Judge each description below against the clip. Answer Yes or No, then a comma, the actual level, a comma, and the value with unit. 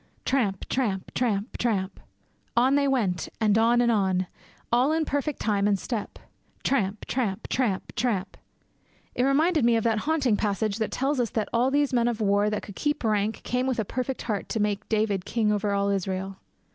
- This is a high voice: Yes, high, 225 Hz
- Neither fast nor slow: Yes, average, 190 wpm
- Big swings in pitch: No, average, 4.0 semitones